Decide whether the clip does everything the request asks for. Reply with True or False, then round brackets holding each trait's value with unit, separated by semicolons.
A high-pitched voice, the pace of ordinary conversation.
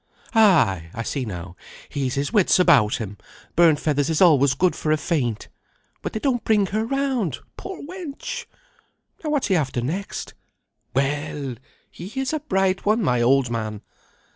False (160 Hz; 165 wpm)